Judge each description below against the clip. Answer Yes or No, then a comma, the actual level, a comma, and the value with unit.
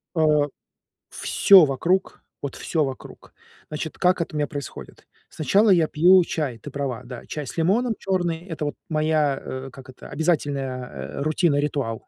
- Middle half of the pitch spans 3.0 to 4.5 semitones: Yes, average, 3.8 semitones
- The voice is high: No, medium, 150 Hz